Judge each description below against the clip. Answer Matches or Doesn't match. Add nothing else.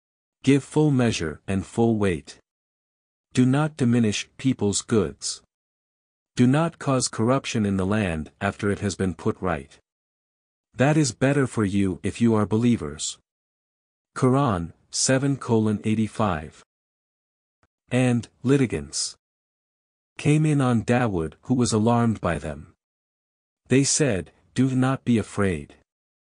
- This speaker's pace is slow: Matches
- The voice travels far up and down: Matches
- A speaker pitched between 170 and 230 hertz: Doesn't match